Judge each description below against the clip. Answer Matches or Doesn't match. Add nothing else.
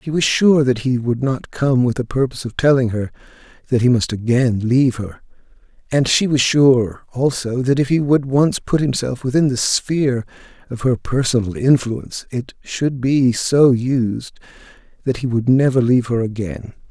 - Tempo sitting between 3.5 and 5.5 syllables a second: Matches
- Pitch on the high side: Doesn't match